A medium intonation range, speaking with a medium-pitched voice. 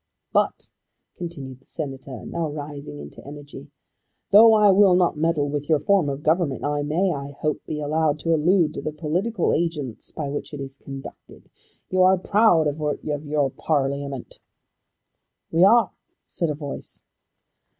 Yes: average, 3.3 semitones; medium, 150 Hz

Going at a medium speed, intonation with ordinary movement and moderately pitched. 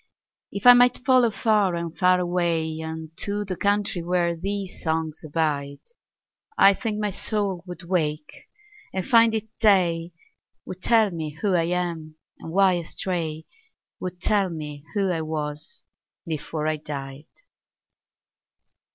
No: slow, 125 wpm; average, 4.0 semitones; medium, 175 Hz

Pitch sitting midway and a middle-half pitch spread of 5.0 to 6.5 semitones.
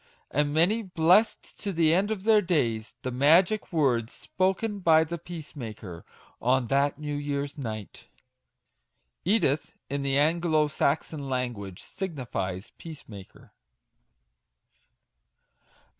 Yes: medium, 145 Hz; wide, 5.5 semitones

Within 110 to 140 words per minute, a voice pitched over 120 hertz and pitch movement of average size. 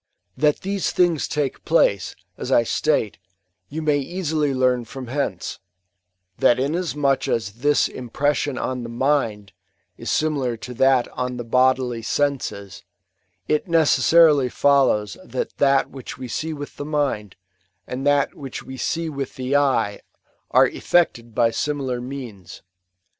Yes: slow, 135 wpm; low, 135 Hz; average, 3.4 semitones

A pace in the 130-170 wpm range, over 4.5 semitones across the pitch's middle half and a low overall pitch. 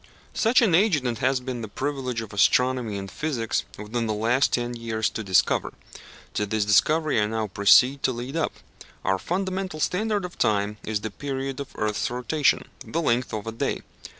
No: average, 190 wpm; average, 5.1 semitones; low, 120 Hz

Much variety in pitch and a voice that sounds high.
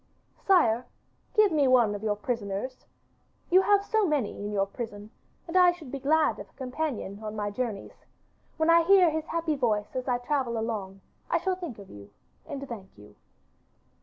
Yes: wide, 7.3 semitones; very high, 255 Hz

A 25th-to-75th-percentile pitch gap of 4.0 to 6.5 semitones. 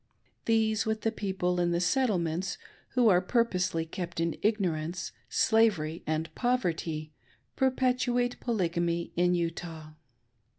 Yes: average, 5.0 semitones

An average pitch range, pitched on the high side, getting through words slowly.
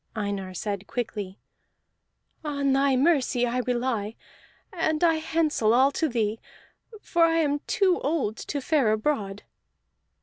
No: wide, 6.0 semitones; very high, 260 Hz; slow, 130 wpm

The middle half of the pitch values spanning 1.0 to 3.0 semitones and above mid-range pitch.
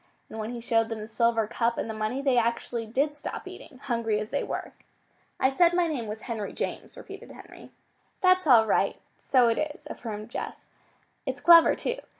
No: average, 4.7 semitones; high, 235 Hz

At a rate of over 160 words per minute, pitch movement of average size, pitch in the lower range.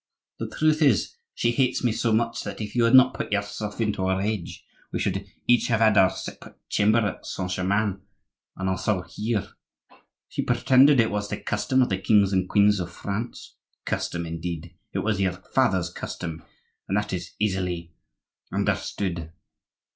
Yes: average, 170 wpm; average, 3.8 semitones; low, 105 Hz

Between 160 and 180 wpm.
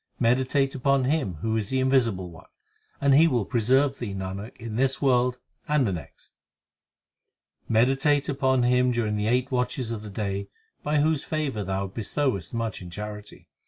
Yes: average, 170 wpm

